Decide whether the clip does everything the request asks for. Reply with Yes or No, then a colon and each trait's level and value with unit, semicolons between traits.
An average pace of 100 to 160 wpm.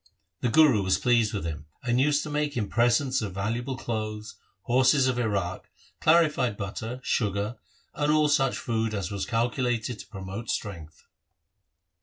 Yes: average, 155 wpm